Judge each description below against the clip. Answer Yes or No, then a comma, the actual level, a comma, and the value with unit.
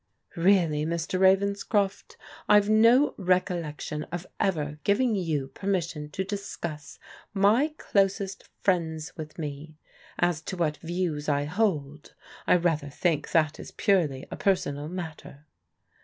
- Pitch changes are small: No, average, 4.5 semitones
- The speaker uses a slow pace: Yes, slow, 130 wpm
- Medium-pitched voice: Yes, medium, 175 Hz